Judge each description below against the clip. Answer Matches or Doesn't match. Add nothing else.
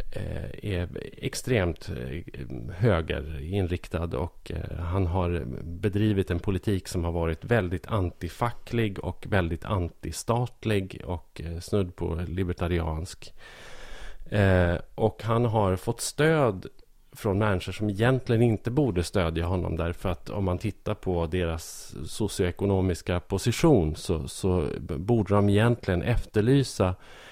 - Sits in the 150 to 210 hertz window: Doesn't match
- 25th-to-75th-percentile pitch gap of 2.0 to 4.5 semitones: Matches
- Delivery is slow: Matches